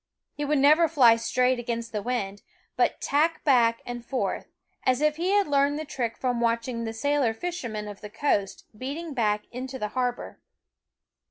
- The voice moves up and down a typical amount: Yes, average, 3.9 semitones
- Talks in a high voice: Yes, very high, 250 Hz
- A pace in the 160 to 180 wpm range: Yes, average, 175 wpm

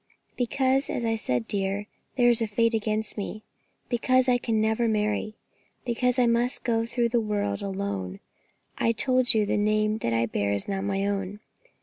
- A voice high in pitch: Yes, high, 220 Hz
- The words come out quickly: No, average, 185 wpm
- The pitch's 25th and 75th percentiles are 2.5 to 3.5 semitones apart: Yes, average, 3.0 semitones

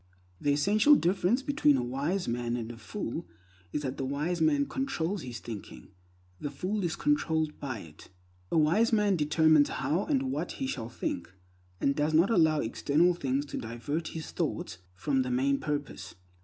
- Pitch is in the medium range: Yes, medium, 150 Hz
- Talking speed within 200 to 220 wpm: No, average, 175 wpm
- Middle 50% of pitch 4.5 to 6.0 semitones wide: Yes, average, 5.3 semitones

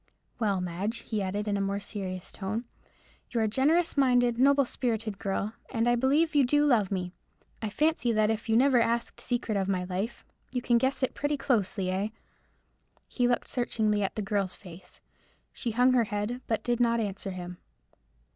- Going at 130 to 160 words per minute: No, average, 190 wpm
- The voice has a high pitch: Yes, high, 225 Hz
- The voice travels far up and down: No, average, 3.8 semitones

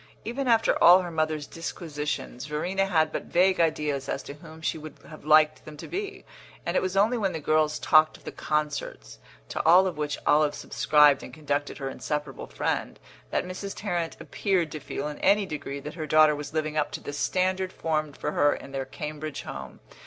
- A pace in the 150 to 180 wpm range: No, fast, 205 wpm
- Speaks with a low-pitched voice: No, medium, 155 Hz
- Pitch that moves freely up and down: No, average, 3.5 semitones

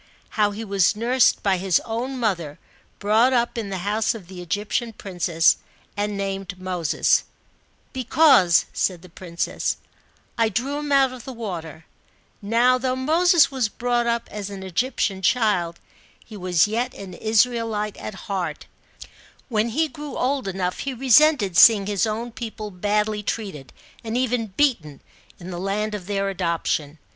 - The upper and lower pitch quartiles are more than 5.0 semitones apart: No, average, 4.5 semitones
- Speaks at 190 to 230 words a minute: No, average, 160 wpm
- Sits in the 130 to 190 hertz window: No, high, 210 Hz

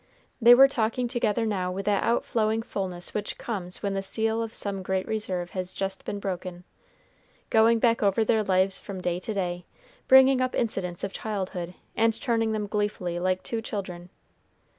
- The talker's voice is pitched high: Yes, high, 205 Hz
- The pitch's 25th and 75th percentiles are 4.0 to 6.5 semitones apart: No, average, 3.3 semitones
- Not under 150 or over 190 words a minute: Yes, average, 175 wpm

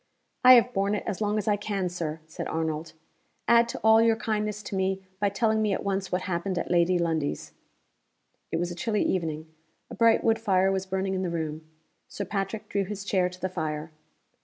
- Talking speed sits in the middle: No, fast, 210 wpm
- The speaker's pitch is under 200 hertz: Yes, high, 190 Hz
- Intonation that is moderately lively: Yes, average, 3.5 semitones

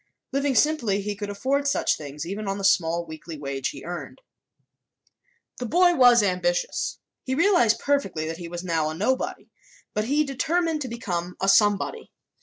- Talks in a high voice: Yes, high, 205 Hz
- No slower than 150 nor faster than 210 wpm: Yes, average, 170 wpm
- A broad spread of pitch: Yes, wide, 8.0 semitones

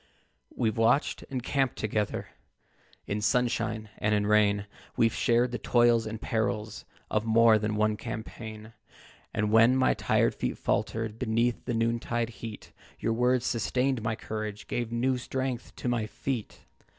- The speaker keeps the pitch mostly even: Yes, narrow, 2.0 semitones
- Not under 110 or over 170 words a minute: Yes, average, 150 wpm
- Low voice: Yes, low, 115 Hz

